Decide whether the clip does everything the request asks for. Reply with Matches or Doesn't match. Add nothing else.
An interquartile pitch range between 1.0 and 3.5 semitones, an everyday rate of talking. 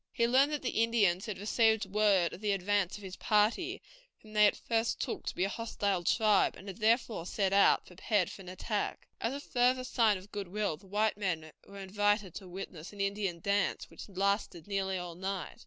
Doesn't match